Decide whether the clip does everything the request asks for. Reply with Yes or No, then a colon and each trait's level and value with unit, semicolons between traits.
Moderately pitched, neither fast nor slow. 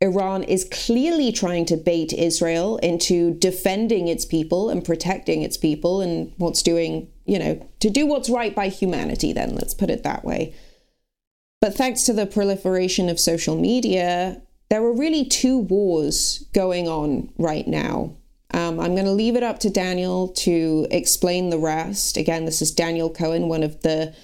Yes: medium, 180 Hz; average, 175 wpm